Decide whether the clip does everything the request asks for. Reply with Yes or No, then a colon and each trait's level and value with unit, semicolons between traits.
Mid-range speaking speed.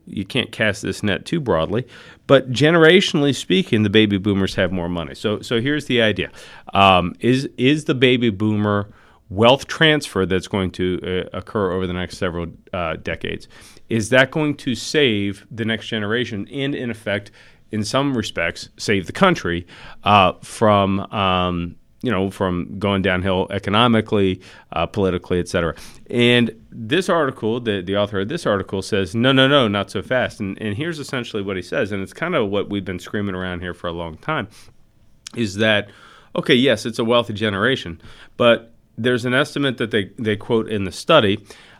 Yes: average, 180 wpm